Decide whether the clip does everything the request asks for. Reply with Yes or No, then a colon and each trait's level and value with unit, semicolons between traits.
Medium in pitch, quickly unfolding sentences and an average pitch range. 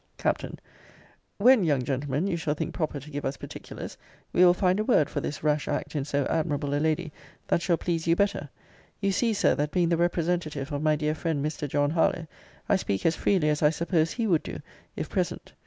Yes: medium, 155 Hz; fast, 220 wpm; average, 3.1 semitones